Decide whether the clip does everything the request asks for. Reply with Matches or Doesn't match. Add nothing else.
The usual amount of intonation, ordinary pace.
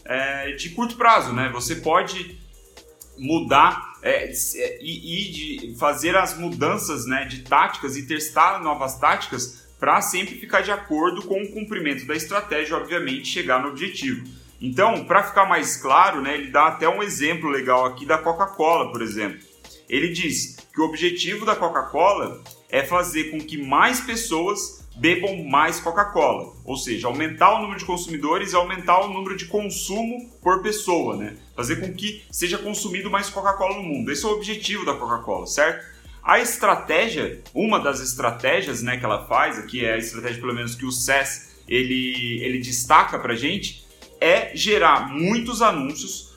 Doesn't match